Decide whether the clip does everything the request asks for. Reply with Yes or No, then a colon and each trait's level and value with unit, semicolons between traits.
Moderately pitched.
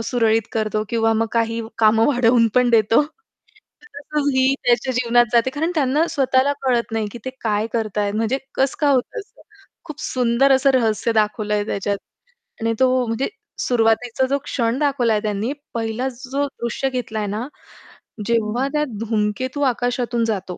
No: high, 235 Hz